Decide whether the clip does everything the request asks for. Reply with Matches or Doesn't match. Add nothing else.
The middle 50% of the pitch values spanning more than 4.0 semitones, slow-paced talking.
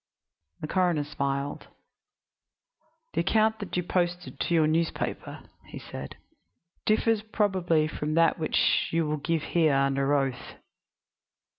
Doesn't match